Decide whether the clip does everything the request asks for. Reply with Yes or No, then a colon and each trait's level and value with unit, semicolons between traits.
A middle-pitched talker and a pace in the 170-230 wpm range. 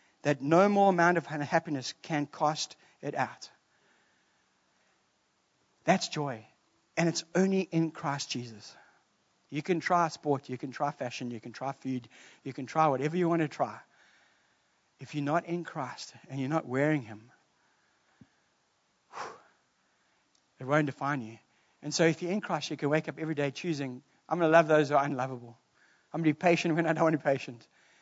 Yes: medium, 150 Hz; average, 180 wpm